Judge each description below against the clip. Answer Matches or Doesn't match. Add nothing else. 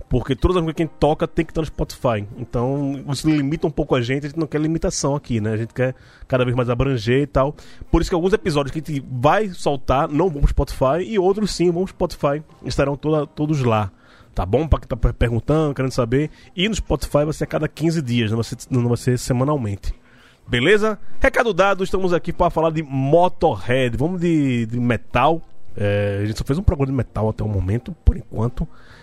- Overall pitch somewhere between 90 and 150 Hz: Matches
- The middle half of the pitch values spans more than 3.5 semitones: Matches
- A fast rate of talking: Matches